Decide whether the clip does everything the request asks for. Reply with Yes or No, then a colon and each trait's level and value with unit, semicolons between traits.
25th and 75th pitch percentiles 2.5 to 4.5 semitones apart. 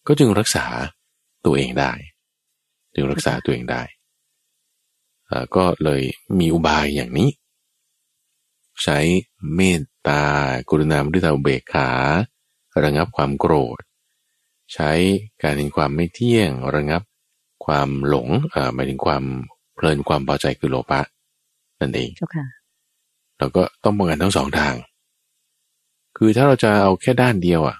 No: average, 4.9 semitones